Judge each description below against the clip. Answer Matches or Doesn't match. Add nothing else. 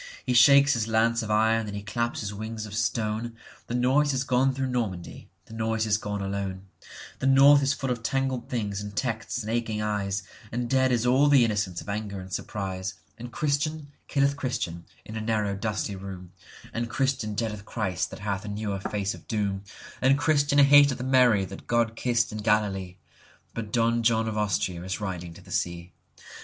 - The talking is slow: Doesn't match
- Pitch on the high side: Doesn't match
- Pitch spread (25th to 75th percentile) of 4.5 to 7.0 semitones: Doesn't match